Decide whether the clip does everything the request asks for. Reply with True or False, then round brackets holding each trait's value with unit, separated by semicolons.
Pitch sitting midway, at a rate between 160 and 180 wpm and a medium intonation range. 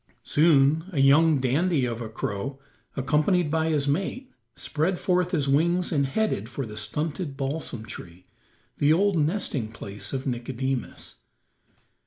False (145 Hz; 140 wpm; 4.3 semitones)